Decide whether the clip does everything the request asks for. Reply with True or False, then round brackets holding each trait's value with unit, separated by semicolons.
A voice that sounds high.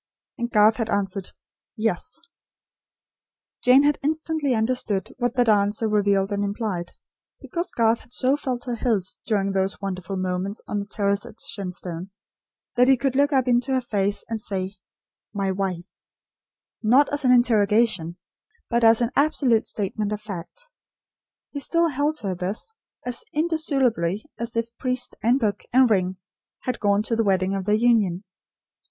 True (220 Hz)